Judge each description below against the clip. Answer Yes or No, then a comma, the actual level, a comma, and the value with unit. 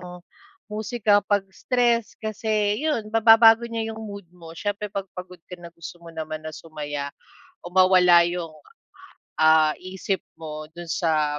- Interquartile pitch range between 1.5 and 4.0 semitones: No, average, 4.7 semitones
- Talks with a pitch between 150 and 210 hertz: Yes, medium, 185 Hz